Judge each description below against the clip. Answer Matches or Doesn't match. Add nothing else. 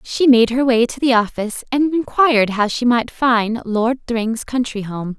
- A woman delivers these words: Matches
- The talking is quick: Doesn't match